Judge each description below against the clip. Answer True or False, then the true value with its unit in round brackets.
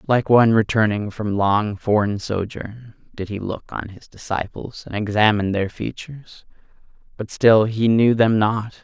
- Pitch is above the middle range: False (110 Hz)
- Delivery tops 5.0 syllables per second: False (4.5 syllables/s)